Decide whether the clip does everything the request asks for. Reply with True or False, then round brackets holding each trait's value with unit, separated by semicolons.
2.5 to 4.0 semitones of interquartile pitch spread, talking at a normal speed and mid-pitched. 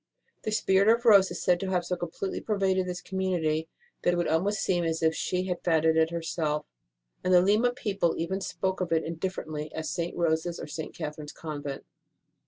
False (2.9 semitones; 210 wpm; 175 Hz)